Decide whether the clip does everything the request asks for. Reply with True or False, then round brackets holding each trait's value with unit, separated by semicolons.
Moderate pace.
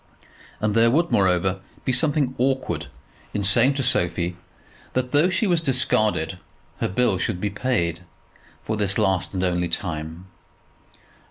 True (145 wpm)